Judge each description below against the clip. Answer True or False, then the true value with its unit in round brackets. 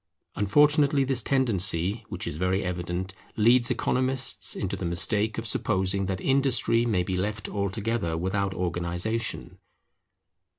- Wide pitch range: False (4.4 semitones)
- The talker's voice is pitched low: True (100 Hz)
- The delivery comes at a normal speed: False (125 wpm)